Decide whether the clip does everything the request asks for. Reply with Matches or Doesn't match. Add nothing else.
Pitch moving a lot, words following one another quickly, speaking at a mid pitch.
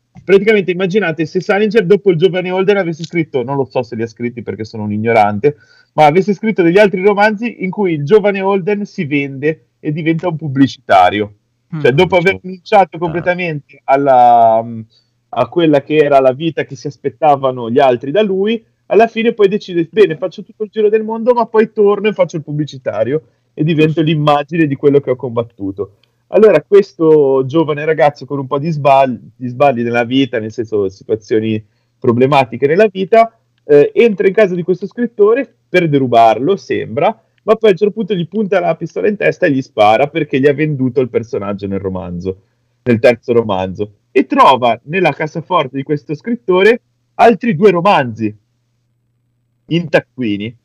Matches